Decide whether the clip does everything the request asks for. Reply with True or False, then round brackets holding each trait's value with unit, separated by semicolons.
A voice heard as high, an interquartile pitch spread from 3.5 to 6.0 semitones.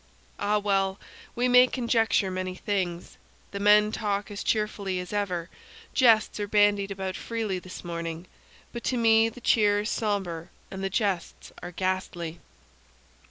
False (200 Hz; 2.5 semitones)